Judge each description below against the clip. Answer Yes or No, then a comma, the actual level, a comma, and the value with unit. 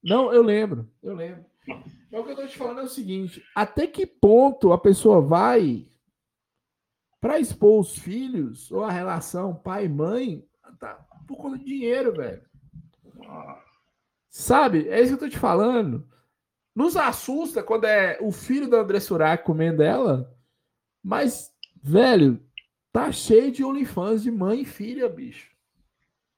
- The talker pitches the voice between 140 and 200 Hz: No, high, 220 Hz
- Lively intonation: Yes, wide, 6.6 semitones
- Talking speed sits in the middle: Yes, average, 150 wpm